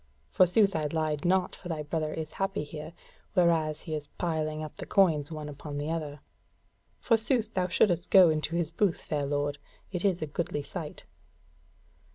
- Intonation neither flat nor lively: Yes, average, 3.0 semitones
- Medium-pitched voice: Yes, medium, 160 Hz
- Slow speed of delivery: No, average, 175 wpm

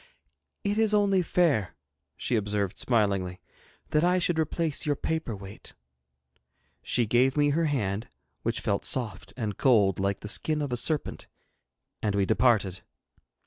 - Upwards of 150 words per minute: No, average, 145 wpm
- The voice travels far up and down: Yes, wide, 7.5 semitones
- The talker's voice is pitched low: Yes, low, 120 Hz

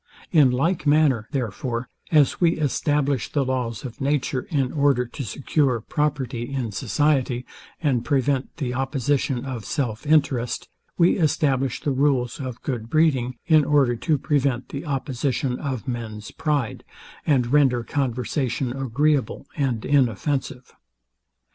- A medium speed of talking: No, slow, 130 wpm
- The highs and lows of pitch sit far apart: No, average, 2.9 semitones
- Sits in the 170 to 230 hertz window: No, low, 135 Hz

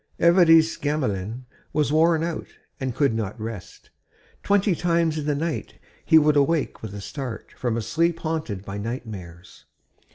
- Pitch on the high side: No, medium, 145 Hz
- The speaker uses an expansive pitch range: Yes, wide, 6.6 semitones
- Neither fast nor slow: Yes, average, 160 wpm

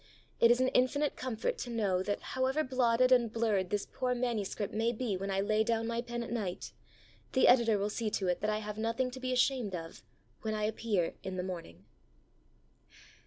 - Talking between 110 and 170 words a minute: No, fast, 205 wpm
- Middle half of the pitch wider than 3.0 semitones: Yes, average, 3.6 semitones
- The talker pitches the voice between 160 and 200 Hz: No, high, 225 Hz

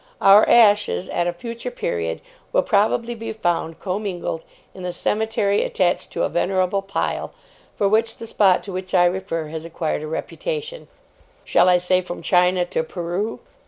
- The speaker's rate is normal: Yes, average, 165 wpm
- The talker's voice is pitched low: No, medium, 185 Hz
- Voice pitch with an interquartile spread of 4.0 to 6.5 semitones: No, average, 3.4 semitones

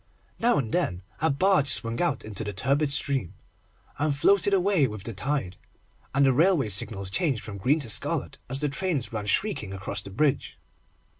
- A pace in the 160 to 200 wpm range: Yes, average, 180 wpm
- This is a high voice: No, low, 135 Hz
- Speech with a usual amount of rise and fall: No, wide, 6.7 semitones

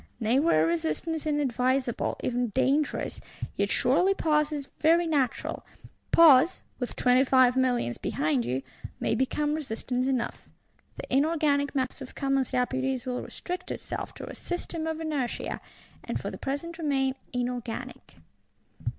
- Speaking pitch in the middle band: No, very high, 265 Hz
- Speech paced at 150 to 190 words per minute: No, slow, 135 wpm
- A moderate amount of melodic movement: Yes, average, 3.4 semitones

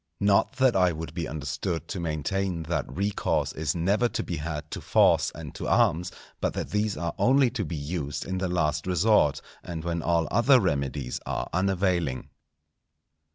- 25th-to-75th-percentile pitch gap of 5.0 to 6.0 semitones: No, average, 4.0 semitones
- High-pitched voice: No, very low, 85 Hz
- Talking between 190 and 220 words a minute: No, average, 175 wpm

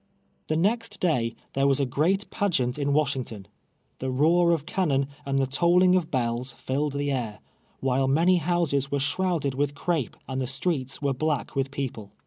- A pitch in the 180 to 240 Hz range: No, medium, 140 Hz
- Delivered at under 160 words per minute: No, average, 180 wpm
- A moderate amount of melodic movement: Yes, average, 4.4 semitones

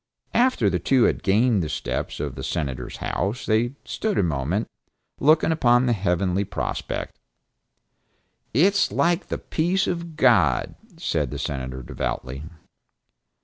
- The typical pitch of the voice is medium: No, low, 105 Hz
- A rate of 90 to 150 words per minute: Yes, average, 140 wpm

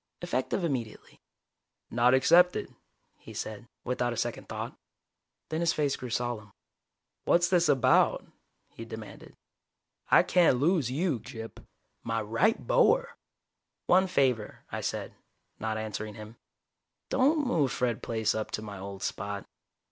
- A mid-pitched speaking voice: No, low, 125 Hz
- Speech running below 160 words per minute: Yes, slow, 135 wpm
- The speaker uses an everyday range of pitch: No, wide, 7.7 semitones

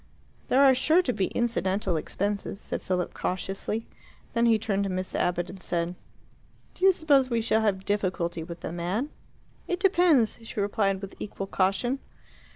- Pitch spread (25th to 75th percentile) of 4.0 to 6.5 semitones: Yes, average, 4.6 semitones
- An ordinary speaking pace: Yes, average, 165 wpm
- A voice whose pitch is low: No, high, 205 Hz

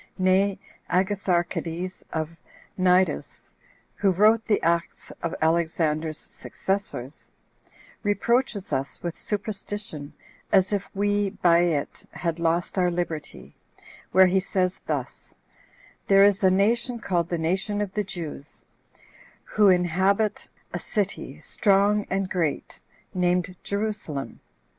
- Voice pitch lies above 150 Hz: Yes, medium, 185 Hz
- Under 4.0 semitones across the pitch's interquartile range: Yes, average, 3.0 semitones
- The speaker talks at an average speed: No, slow, 115 wpm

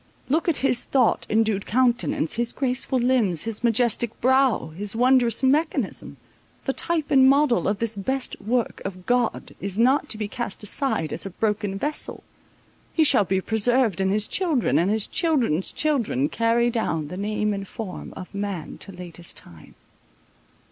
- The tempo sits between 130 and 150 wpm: No, average, 160 wpm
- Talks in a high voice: Yes, high, 225 Hz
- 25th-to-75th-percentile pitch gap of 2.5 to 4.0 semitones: No, average, 4.7 semitones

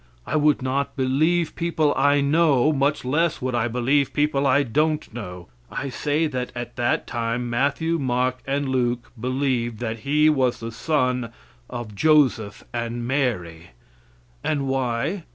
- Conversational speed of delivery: Yes, average, 150 wpm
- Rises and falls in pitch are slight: No, average, 3.5 semitones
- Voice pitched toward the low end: Yes, low, 130 Hz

